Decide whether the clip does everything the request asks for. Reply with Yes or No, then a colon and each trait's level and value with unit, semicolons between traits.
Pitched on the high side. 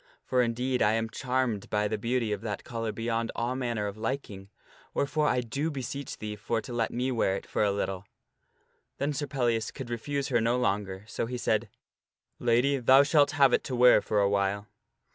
No: low, 120 Hz